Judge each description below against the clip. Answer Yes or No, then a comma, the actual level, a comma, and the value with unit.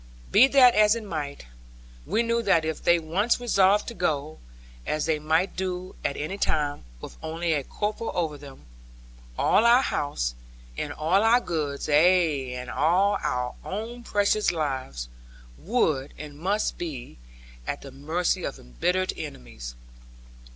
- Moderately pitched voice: Yes, medium, 165 Hz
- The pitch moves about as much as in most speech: No, wide, 5.9 semitones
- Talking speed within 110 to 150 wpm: Yes, average, 145 wpm